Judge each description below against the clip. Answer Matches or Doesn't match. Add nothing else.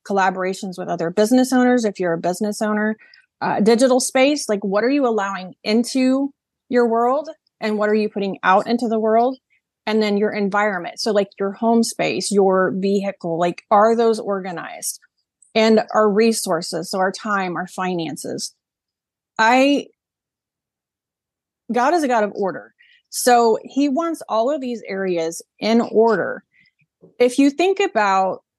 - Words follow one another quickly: Doesn't match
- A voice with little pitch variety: Doesn't match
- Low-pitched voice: Doesn't match